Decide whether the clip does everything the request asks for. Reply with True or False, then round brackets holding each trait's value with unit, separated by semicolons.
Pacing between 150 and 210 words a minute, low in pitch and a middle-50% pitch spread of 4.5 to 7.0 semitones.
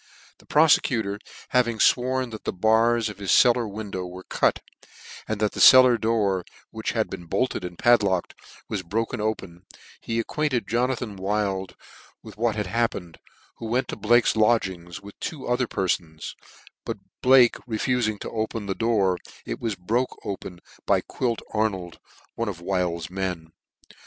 False (160 wpm; 110 Hz; 4.0 semitones)